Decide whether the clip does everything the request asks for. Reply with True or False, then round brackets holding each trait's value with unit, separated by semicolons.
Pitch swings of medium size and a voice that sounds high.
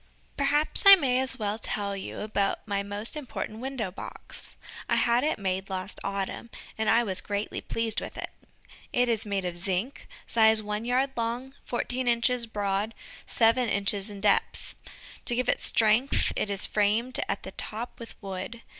True (3.4 semitones; 220 Hz)